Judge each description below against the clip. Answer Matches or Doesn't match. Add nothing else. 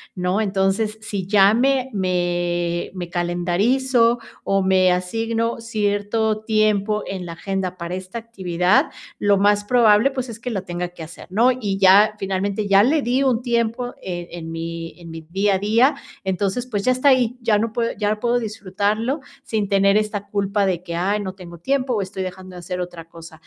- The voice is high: Matches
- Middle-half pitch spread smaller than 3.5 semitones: Doesn't match